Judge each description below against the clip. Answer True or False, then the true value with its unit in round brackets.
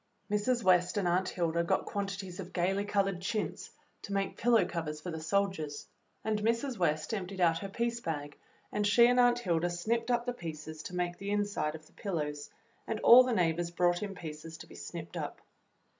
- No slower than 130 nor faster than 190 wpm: False (200 wpm)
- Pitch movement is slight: False (3.9 semitones)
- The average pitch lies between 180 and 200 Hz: True (185 Hz)